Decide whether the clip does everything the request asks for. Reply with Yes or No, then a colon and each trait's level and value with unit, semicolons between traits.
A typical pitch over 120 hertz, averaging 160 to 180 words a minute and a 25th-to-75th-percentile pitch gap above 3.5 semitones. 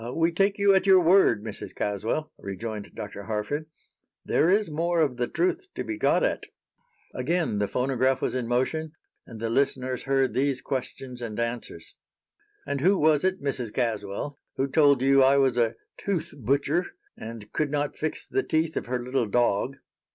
Yes: low, 135 Hz; average, 175 wpm; average, 5.1 semitones